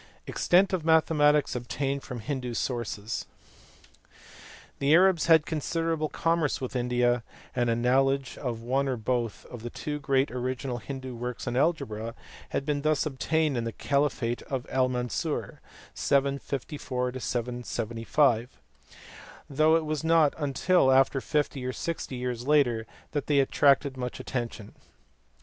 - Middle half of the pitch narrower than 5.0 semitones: Yes, average, 3.3 semitones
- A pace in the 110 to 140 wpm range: Yes, slow, 135 wpm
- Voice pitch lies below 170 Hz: Yes, low, 135 Hz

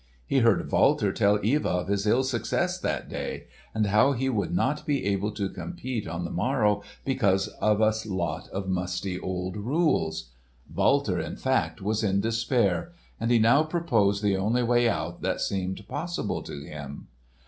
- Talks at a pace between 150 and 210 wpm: Yes, average, 170 wpm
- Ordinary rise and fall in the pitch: Yes, average, 4.5 semitones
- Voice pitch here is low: Yes, low, 105 Hz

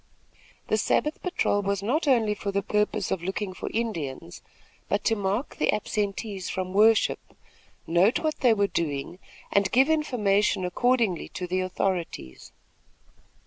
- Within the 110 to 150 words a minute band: Yes, average, 145 wpm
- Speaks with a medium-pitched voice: No, high, 200 Hz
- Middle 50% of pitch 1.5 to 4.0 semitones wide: Yes, average, 3.3 semitones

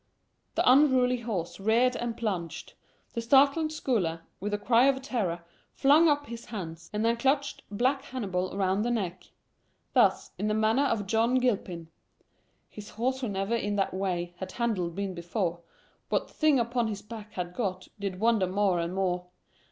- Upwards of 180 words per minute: No, average, 170 wpm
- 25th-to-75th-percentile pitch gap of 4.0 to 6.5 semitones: Yes, average, 4.9 semitones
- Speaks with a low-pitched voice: No, high, 215 Hz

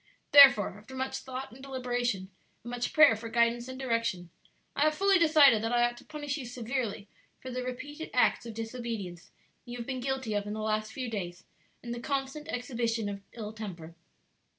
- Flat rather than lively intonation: No, average, 3.3 semitones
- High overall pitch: Yes, high, 240 Hz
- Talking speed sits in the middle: Yes, average, 195 wpm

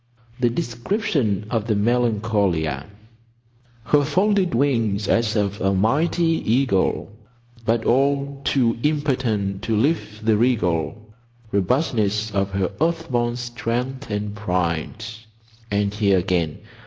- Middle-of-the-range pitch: No, low, 115 Hz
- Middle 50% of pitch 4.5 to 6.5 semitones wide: Yes, average, 4.8 semitones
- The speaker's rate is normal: No, slow, 115 wpm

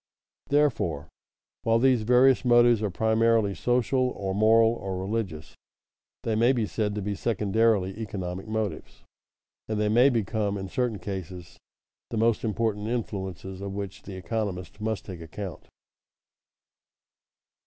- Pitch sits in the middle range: No, low, 105 Hz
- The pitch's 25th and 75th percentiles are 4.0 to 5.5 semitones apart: No, average, 3.1 semitones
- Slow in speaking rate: Yes, slow, 130 wpm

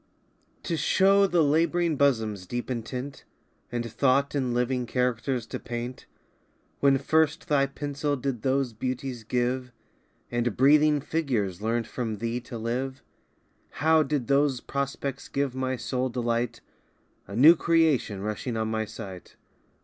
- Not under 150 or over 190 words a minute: No, slow, 135 wpm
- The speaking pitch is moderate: No, low, 130 Hz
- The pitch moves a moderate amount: Yes, average, 3.2 semitones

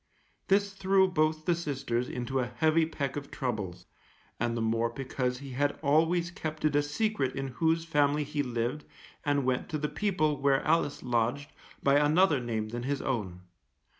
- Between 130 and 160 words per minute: No, average, 175 wpm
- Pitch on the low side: No, medium, 145 Hz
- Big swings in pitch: No, average, 4.0 semitones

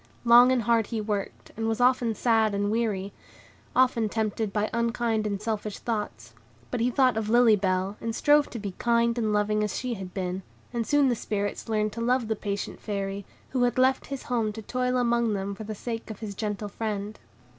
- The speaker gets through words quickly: Yes, fast, 210 wpm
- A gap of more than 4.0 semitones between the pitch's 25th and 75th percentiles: No, narrow, 2.5 semitones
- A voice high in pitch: Yes, high, 220 Hz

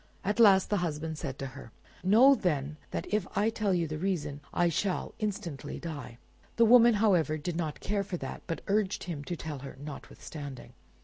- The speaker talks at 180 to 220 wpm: Yes, average, 190 wpm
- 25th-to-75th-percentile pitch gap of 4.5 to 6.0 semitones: Yes, average, 5.3 semitones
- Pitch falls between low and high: Yes, medium, 175 Hz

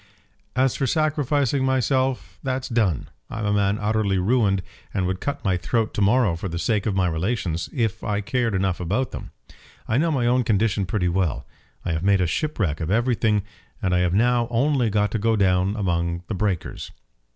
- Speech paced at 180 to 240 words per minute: Yes, average, 190 wpm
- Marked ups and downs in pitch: No, average, 4.8 semitones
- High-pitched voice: No, low, 105 Hz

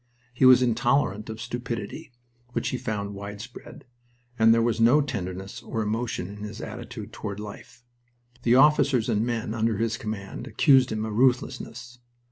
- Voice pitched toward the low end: Yes, low, 115 Hz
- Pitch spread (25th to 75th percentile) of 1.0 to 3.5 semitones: Yes, average, 2.7 semitones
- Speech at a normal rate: Yes, average, 155 wpm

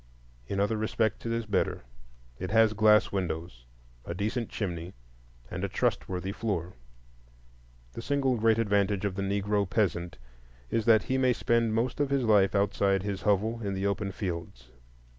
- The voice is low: Yes, low, 100 Hz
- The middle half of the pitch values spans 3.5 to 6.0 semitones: No, average, 2.8 semitones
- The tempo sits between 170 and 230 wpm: No, average, 160 wpm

